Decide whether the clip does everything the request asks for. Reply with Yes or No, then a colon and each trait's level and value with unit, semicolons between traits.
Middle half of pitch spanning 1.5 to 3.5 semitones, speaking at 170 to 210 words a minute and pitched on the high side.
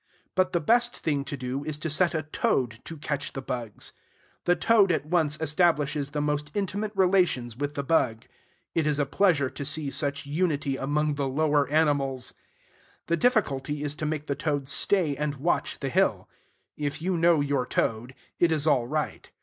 No: average, 2.8 semitones; average, 185 wpm; medium, 150 Hz